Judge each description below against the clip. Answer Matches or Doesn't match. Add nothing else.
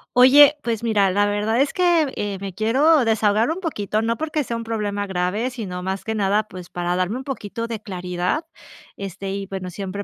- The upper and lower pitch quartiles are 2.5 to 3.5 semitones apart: Doesn't match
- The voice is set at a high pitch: Matches